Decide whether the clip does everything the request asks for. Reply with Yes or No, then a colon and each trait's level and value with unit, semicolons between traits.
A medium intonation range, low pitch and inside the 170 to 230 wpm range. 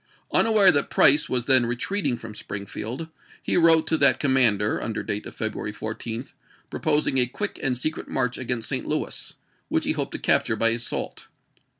Yes: average, 4.4 semitones; low, 125 Hz; average, 175 wpm